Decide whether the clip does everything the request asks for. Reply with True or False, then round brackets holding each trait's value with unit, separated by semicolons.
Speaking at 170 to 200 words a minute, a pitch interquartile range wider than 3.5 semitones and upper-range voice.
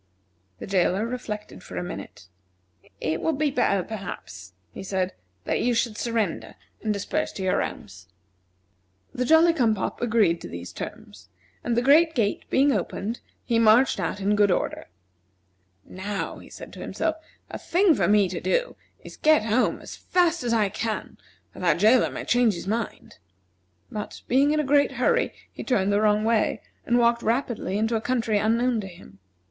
True (180 wpm; 4.4 semitones; 220 Hz)